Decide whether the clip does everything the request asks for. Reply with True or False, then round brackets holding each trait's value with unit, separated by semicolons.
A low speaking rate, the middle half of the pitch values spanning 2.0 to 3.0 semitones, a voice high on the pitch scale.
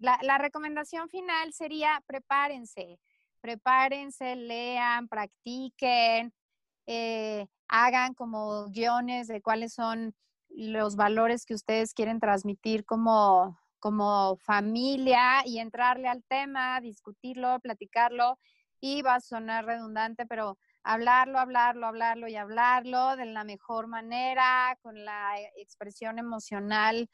True (110 wpm; 2.6 semitones; 235 Hz)